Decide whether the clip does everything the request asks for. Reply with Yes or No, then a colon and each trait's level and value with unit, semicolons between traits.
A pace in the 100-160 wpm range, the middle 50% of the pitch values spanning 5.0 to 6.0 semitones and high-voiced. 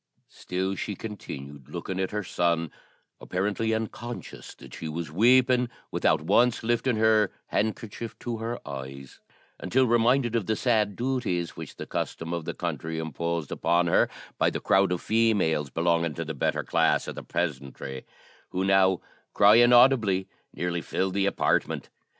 No: average, 155 wpm; average, 5.3 semitones; very low, 95 Hz